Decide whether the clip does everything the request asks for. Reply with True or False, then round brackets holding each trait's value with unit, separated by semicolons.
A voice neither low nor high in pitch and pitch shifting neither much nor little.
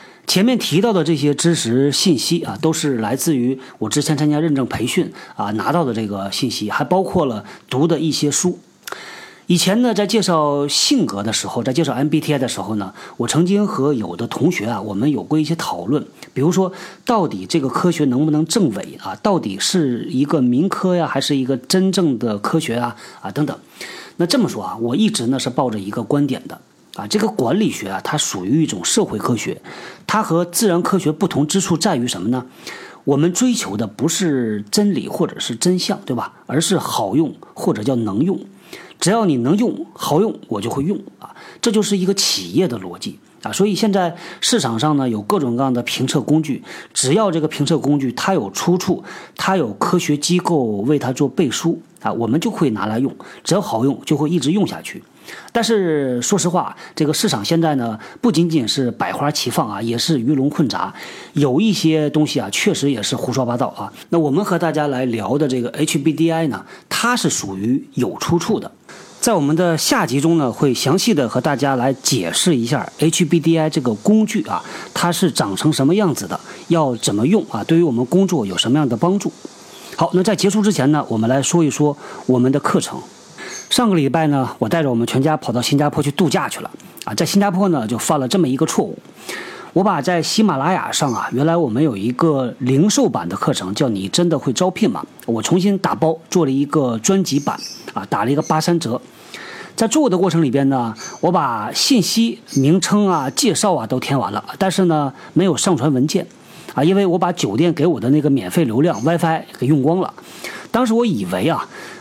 True (155 Hz; 5.0 semitones)